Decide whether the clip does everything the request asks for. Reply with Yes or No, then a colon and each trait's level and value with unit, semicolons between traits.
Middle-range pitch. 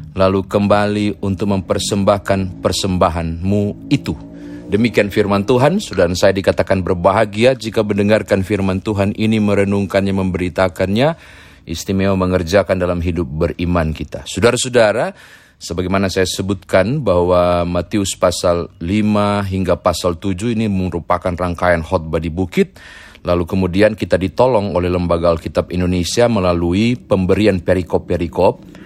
No: very low, 95 Hz